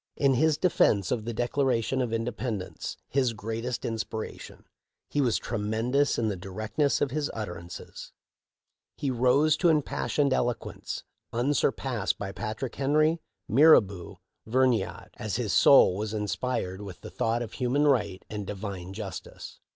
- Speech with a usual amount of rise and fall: Yes, average, 4.4 semitones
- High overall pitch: No, low, 120 Hz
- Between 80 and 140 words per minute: No, average, 150 wpm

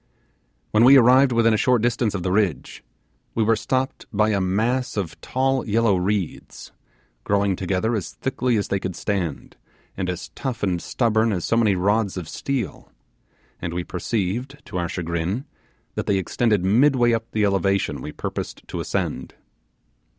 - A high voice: No, low, 105 Hz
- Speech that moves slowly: No, average, 165 wpm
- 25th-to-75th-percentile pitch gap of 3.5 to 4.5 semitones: Yes, average, 4.2 semitones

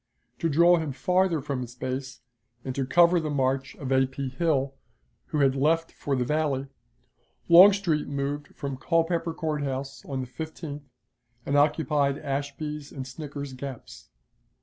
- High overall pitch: No, medium, 140 Hz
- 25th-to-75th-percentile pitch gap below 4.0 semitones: Yes, average, 3.0 semitones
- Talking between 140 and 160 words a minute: Yes, average, 150 wpm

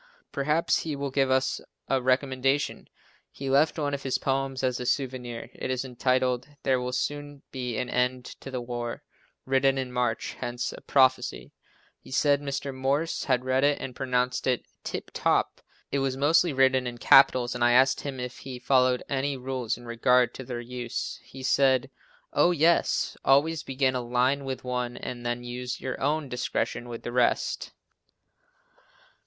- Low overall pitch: Yes, low, 130 Hz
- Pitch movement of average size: No, narrow, 1.7 semitones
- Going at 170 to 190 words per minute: Yes, average, 175 wpm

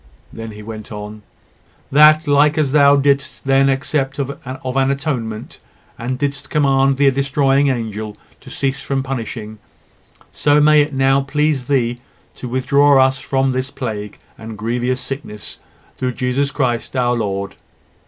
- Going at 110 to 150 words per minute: Yes, average, 145 wpm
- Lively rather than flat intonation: No, average, 2.9 semitones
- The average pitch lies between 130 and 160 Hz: Yes, low, 135 Hz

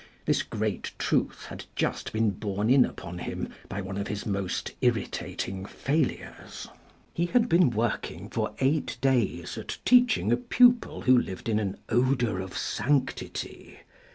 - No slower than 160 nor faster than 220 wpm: No, average, 150 wpm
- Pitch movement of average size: No, wide, 5.8 semitones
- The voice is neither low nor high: No, low, 115 Hz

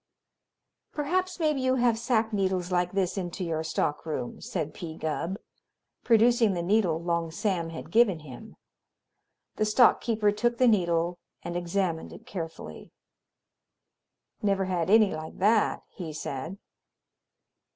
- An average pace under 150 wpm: Yes, slow, 135 wpm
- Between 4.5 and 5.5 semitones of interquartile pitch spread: Yes, average, 5.0 semitones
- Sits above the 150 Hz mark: Yes, high, 190 Hz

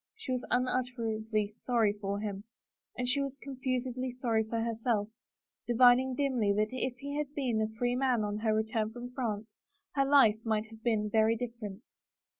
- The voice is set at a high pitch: Yes, high, 235 Hz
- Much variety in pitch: No, average, 2.7 semitones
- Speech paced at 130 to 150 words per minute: No, average, 165 wpm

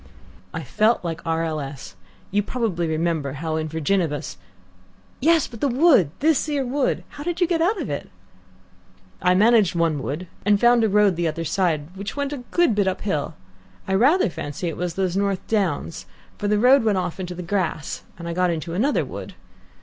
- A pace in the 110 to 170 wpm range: No, average, 195 wpm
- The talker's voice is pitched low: No, high, 190 Hz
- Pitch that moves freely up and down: Yes, wide, 6.3 semitones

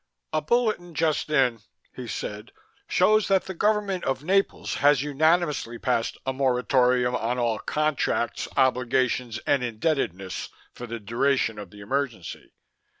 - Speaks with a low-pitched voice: Yes, low, 130 Hz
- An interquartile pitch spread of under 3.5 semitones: No, average, 4.8 semitones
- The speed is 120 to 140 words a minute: Yes, slow, 135 wpm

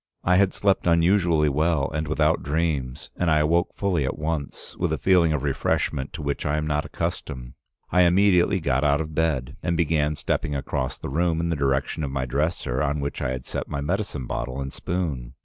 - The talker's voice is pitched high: No, very low, 75 Hz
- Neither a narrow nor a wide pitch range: Yes, average, 3.5 semitones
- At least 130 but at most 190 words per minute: No, fast, 205 wpm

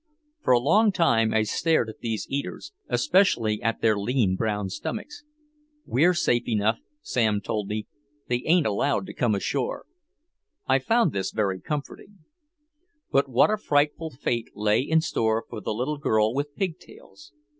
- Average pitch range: No, wide, 5.9 semitones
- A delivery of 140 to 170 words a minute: Yes, average, 160 wpm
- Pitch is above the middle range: No, low, 120 Hz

